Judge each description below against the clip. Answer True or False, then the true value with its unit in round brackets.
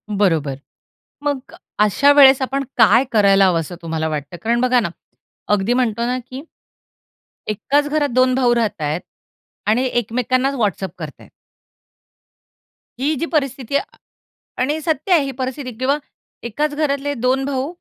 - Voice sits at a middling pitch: False (255 Hz)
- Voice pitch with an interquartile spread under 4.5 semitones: False (4.8 semitones)